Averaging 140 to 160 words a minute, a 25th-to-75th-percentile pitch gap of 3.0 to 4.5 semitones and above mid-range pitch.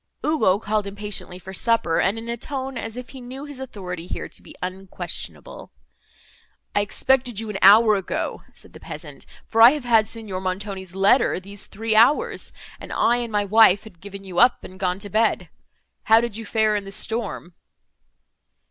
No: average, 185 wpm; average, 3.4 semitones; high, 215 Hz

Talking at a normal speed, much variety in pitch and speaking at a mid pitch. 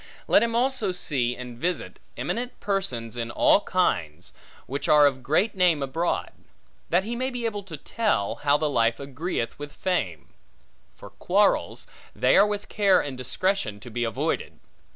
Yes: average, 170 wpm; wide, 8.1 semitones; medium, 150 Hz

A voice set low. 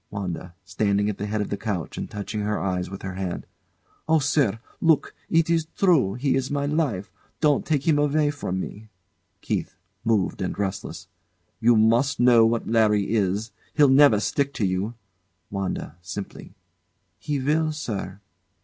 Yes: low, 110 Hz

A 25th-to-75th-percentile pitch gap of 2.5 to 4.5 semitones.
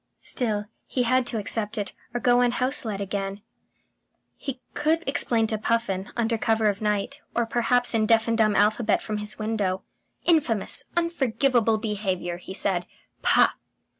Yes: average, 2.8 semitones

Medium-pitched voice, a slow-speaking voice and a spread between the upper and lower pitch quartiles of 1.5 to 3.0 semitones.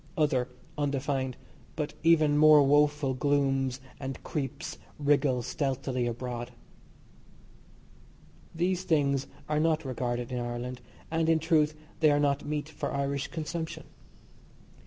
Yes: medium, 145 Hz; slow, 115 wpm; average, 2.7 semitones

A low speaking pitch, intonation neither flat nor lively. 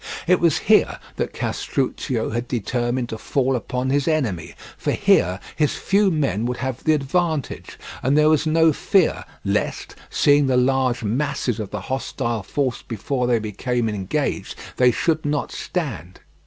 Yes: low, 130 Hz; average, 4.1 semitones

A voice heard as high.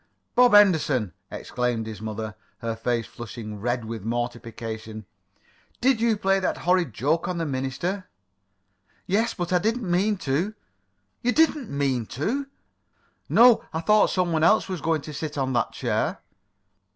No: medium, 155 Hz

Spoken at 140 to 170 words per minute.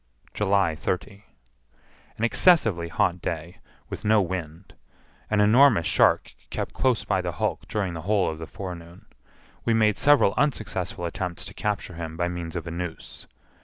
Yes: average, 160 wpm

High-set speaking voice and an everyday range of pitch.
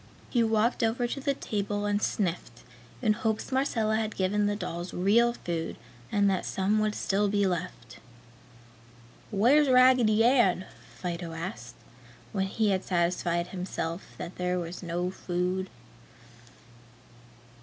Yes: high, 195 Hz; average, 3.6 semitones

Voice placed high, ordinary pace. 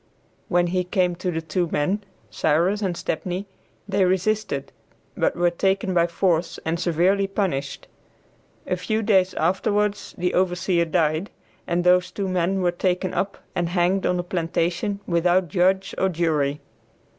No: medium, 180 Hz; average, 150 wpm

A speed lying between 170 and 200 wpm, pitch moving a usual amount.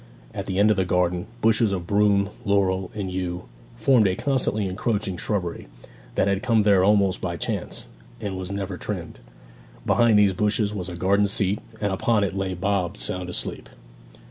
No: average, 175 wpm; narrow, 2.1 semitones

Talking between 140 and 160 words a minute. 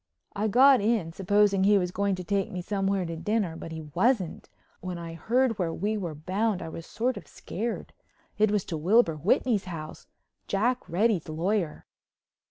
No: average, 175 wpm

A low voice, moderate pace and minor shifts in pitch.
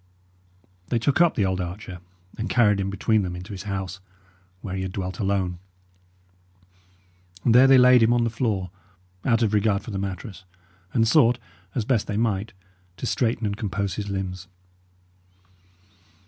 No: low, 105 Hz; average, 165 wpm; average, 3.3 semitones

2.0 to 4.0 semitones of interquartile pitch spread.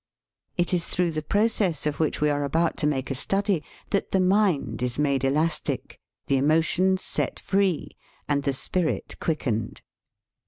No: average, 4.6 semitones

